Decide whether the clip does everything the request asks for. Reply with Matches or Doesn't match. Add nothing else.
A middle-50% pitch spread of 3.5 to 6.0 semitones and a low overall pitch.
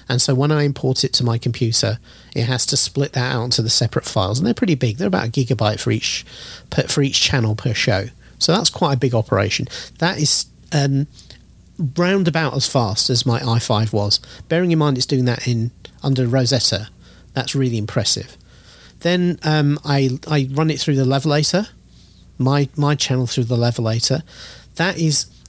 Matches